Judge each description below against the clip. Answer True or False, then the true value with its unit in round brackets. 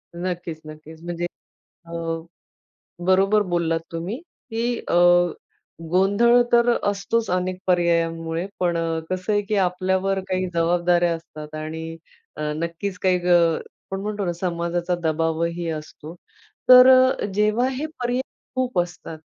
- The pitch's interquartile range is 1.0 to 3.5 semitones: True (3.0 semitones)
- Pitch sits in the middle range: True (180 Hz)